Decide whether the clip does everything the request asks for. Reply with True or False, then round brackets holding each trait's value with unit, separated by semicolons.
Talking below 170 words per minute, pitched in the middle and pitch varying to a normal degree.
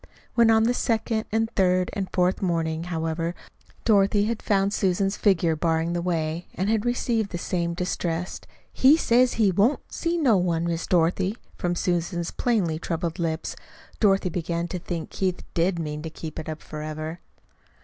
False (175 wpm; 180 Hz; 3.7 semitones)